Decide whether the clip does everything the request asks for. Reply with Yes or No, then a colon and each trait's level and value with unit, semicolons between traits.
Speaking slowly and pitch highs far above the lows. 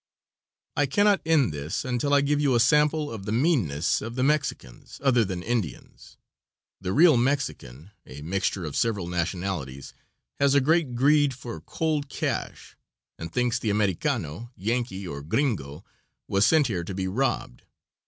No: average, 155 wpm; wide, 8.0 semitones